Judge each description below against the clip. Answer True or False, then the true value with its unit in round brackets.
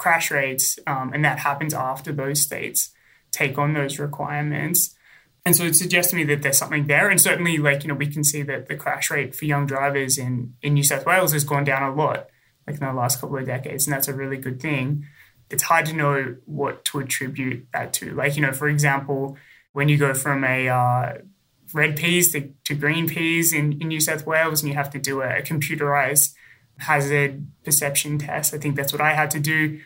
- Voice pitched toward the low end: False (145 Hz)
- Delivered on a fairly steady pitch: True (1.8 semitones)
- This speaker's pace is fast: True (225 wpm)